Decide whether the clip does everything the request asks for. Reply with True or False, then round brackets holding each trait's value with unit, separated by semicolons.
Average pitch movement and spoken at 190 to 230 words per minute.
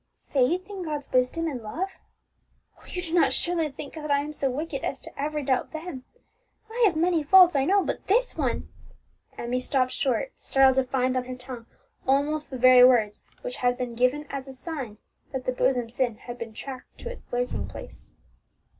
True (4.1 semitones; 200 wpm)